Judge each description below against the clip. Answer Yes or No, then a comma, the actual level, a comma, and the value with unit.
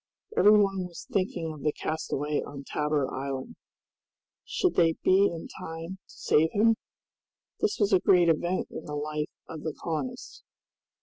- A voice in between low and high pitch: Yes, medium, 165 Hz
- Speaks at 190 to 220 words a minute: No, average, 160 wpm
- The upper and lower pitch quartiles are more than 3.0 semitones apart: Yes, average, 3.9 semitones